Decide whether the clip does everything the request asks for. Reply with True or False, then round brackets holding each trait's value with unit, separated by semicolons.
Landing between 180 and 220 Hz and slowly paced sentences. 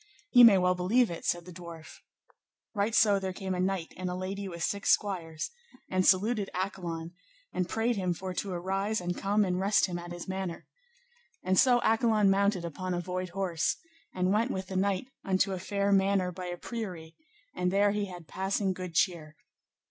False (185 Hz; 195 wpm)